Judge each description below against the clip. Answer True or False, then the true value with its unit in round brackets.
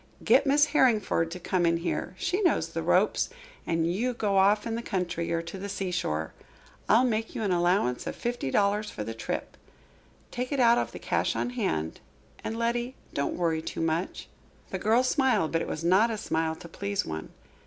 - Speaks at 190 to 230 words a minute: True (200 wpm)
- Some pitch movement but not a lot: False (5.9 semitones)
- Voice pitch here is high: True (195 Hz)